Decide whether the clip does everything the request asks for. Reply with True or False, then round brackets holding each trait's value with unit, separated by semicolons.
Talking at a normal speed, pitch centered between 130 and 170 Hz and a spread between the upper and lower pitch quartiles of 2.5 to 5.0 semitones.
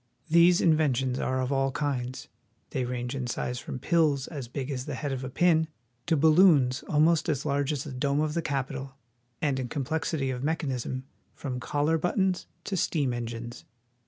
True (185 wpm; 140 Hz; 3.4 semitones)